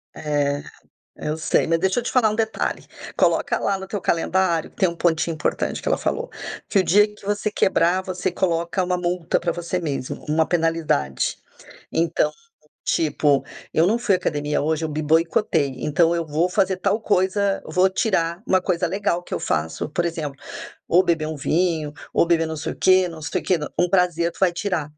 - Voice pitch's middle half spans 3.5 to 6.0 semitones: No, average, 3.0 semitones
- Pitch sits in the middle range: Yes, medium, 170 Hz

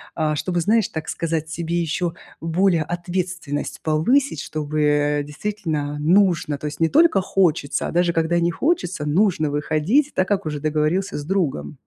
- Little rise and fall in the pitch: No, average, 3.7 semitones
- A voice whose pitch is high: No, medium, 165 Hz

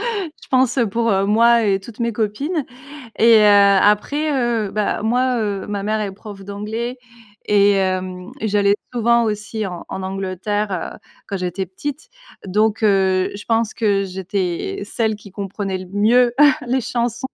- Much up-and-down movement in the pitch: No, average, 3.2 semitones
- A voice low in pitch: No, high, 210 Hz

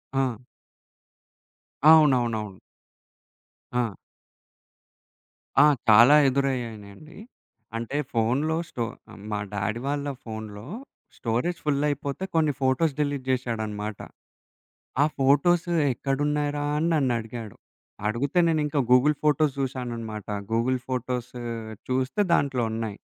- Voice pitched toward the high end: No, low, 130 Hz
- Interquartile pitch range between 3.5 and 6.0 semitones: Yes, average, 4.3 semitones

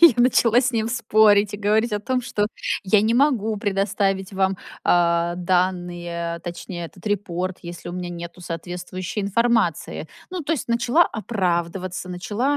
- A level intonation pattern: No, average, 4.2 semitones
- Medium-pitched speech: No, high, 195 Hz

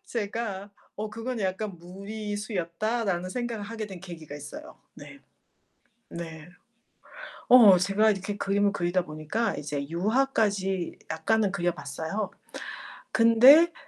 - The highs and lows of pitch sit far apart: No, average, 4.1 semitones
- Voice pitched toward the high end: Yes, high, 200 Hz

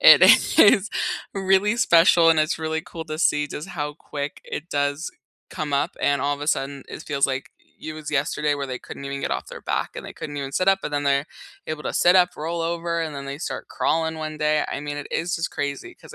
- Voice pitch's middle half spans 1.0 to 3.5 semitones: Yes, narrow, 2.6 semitones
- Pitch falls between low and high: Yes, medium, 150 Hz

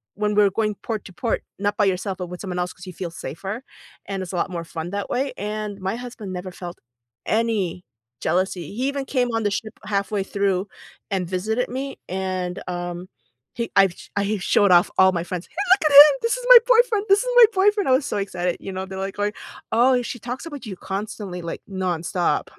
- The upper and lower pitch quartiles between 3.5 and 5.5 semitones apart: Yes, average, 4.4 semitones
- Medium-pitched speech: No, high, 200 Hz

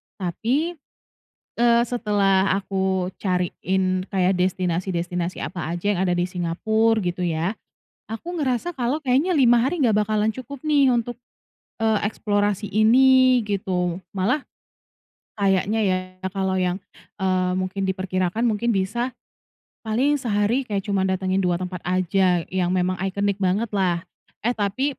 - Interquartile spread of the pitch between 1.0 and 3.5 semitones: No, average, 4.1 semitones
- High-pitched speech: Yes, high, 195 Hz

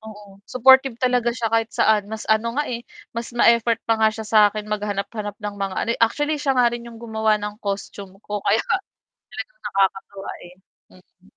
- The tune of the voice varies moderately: No, narrow, 2.3 semitones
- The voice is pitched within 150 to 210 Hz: No, high, 220 Hz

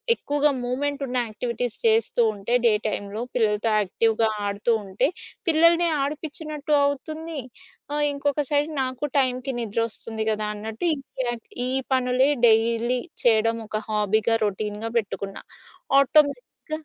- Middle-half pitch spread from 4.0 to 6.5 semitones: Yes, average, 4.8 semitones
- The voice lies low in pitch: No, high, 245 Hz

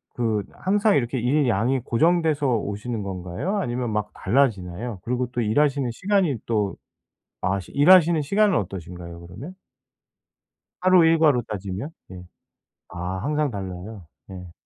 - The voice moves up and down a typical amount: No, wide, 7.5 semitones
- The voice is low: Yes, low, 120 Hz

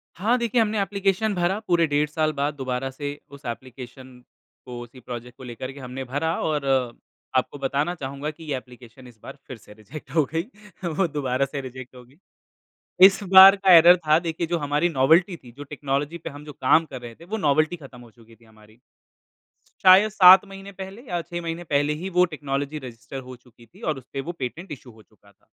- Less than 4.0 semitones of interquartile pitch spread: No, average, 5.1 semitones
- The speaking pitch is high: No, medium, 145 Hz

